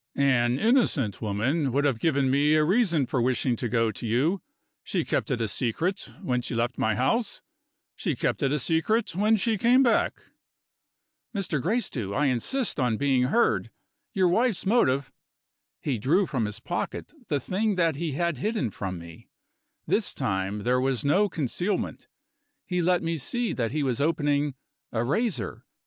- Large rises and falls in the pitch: Yes, wide, 7.1 semitones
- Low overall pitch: No, medium, 145 Hz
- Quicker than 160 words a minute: Yes, average, 170 wpm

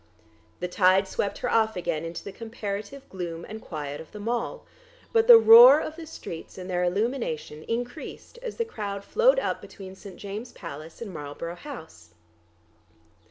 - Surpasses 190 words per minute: No, average, 165 wpm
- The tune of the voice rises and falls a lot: Yes, wide, 6.3 semitones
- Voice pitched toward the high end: Yes, high, 200 Hz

